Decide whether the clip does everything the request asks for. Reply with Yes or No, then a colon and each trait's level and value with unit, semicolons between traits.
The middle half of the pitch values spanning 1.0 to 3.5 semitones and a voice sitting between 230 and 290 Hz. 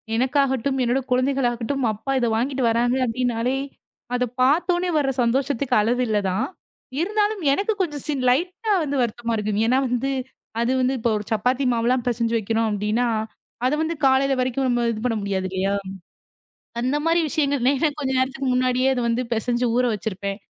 Yes: average, 3.0 semitones; very high, 250 Hz